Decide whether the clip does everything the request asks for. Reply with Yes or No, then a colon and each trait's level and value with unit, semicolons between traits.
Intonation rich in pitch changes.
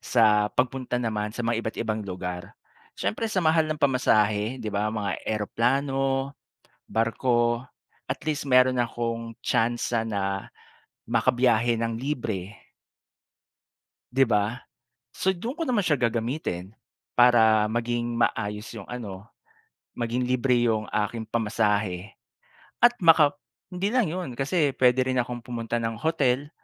No: average, 3.6 semitones